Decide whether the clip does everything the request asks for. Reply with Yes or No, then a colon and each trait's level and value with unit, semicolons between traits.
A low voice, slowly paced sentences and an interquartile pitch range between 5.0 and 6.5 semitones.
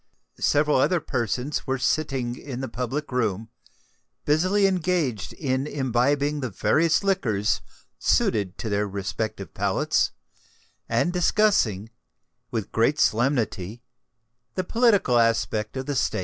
Yes: low, 130 Hz; slow, 120 wpm; wide, 5.4 semitones